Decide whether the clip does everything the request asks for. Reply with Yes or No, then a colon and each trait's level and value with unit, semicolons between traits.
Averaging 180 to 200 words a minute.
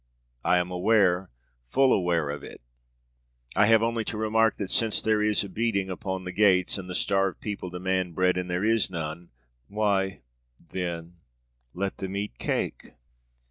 No: average, 165 wpm